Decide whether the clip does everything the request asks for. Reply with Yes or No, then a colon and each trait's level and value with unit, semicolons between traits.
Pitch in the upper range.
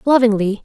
Yes: high, 225 Hz